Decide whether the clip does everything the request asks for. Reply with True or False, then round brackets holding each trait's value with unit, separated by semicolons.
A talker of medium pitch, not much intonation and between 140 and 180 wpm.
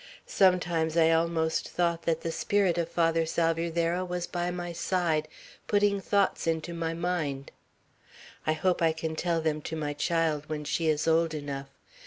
True (165 Hz; 1.6 semitones; 165 wpm)